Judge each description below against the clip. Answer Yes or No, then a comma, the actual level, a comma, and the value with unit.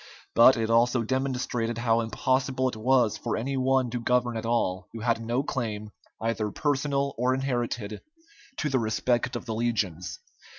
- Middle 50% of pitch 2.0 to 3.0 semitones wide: Yes, narrow, 2.4 semitones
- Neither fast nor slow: Yes, average, 165 wpm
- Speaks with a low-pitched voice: Yes, low, 120 Hz